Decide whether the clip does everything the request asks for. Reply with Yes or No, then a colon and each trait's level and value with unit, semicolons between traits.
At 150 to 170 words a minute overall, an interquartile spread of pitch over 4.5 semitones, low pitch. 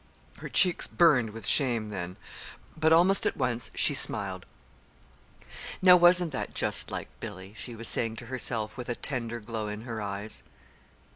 Yes: average, 160 wpm; wide, 5.6 semitones; low, 115 Hz